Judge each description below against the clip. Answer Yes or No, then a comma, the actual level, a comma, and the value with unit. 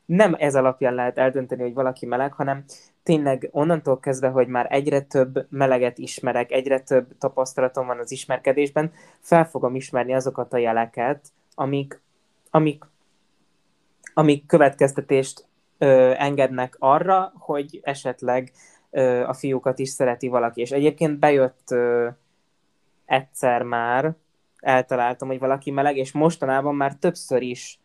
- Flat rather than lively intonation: Yes, narrow, 2.2 semitones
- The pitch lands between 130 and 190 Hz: Yes, low, 135 Hz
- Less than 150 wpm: Yes, average, 130 wpm